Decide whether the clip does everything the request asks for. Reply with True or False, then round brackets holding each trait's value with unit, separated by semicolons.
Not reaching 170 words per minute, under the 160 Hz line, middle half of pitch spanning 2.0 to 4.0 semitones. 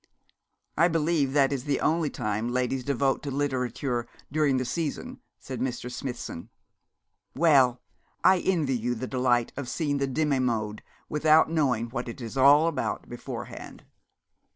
True (150 wpm; 135 Hz; 3.4 semitones)